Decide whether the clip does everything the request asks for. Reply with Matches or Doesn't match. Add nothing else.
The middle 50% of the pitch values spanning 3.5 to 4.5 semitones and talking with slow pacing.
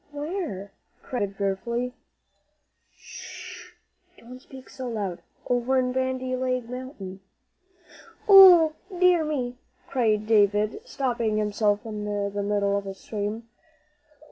Matches